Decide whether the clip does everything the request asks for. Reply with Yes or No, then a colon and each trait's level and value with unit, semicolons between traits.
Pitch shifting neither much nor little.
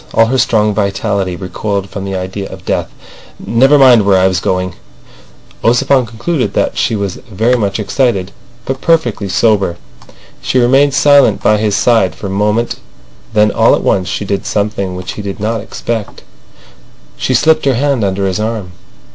Yes: average, 3.6 semitones